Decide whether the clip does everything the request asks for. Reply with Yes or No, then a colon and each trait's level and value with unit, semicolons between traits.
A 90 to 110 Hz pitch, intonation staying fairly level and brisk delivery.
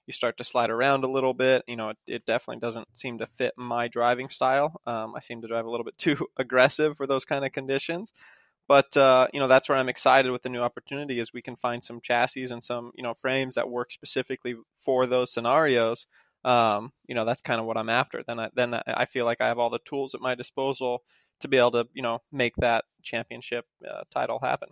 No: low, 125 Hz; narrow, 2.0 semitones; fast, 240 wpm